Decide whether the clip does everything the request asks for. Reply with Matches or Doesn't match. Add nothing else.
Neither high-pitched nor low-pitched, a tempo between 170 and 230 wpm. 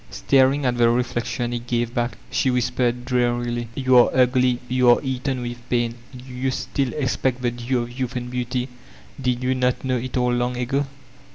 Doesn't match